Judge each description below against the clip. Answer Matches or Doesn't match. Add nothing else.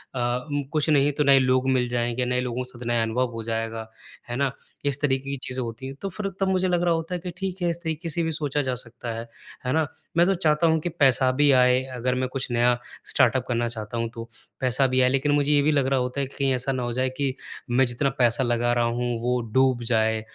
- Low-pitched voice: Matches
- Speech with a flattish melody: Doesn't match